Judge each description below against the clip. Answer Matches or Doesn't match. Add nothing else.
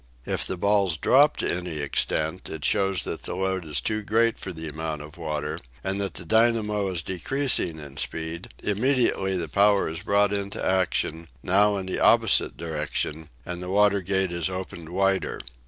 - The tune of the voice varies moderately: Matches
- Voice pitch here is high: Doesn't match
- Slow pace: Doesn't match